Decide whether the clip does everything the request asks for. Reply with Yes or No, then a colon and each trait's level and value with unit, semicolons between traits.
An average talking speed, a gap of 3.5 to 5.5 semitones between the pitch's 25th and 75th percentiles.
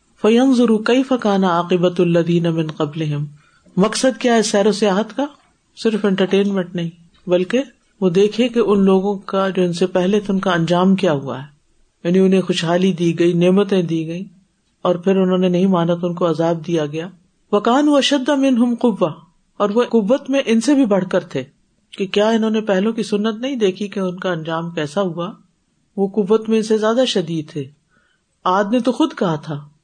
No: fast, 195 wpm; average, 4.1 semitones